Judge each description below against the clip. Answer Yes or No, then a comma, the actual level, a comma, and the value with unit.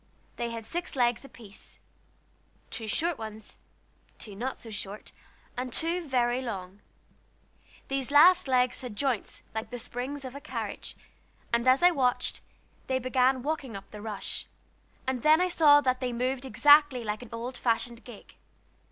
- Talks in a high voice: Yes, very high, 250 Hz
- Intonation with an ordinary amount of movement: Yes, average, 3.1 semitones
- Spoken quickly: No, average, 160 wpm